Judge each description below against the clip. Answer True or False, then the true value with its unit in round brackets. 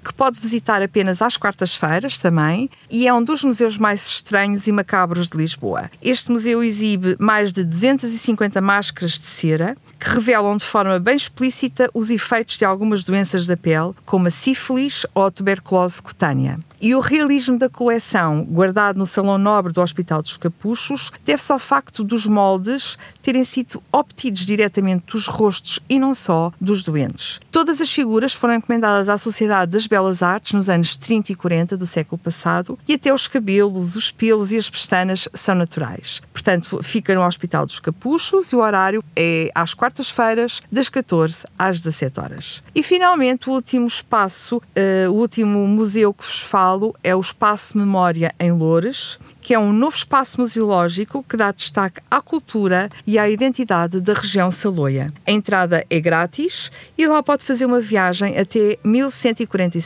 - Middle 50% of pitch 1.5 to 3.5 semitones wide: False (4.7 semitones)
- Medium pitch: False (205 Hz)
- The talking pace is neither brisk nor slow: True (170 wpm)